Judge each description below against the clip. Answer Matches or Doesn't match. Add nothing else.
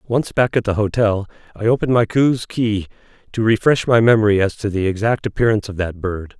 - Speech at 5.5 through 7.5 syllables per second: Matches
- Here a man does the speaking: Matches